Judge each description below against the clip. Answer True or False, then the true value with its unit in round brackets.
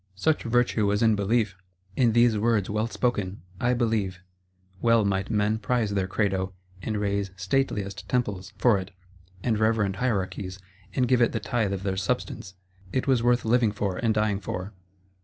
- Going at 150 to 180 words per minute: True (170 wpm)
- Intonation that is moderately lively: True (3.2 semitones)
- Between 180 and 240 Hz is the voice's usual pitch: False (105 Hz)